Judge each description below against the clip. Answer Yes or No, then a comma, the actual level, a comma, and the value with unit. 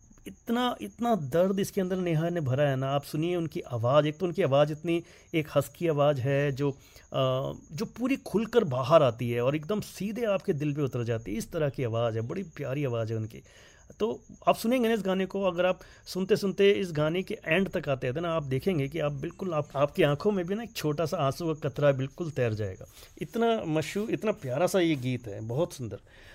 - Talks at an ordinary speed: No, fast, 225 wpm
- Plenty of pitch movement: Yes, wide, 6.0 semitones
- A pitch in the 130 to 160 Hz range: Yes, medium, 155 Hz